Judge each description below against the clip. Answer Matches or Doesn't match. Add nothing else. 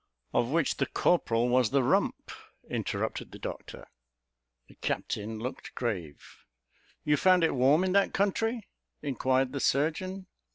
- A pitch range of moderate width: Doesn't match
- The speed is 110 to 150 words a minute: Matches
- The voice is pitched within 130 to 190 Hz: Matches